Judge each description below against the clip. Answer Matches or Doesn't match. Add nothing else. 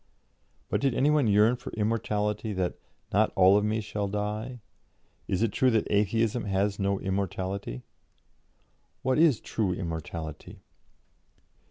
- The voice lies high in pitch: Doesn't match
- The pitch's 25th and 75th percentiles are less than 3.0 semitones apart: Matches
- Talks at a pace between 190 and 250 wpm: Doesn't match